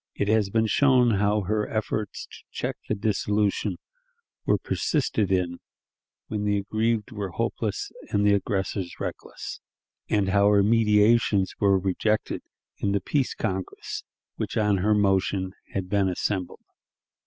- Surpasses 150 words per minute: No, slow, 135 wpm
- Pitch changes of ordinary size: No, narrow, 1.9 semitones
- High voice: No, low, 105 Hz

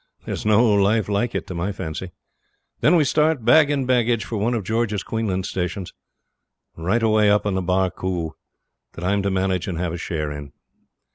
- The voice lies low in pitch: Yes, low, 100 Hz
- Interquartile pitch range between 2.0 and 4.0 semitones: Yes, average, 3.7 semitones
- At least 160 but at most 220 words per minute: Yes, average, 190 wpm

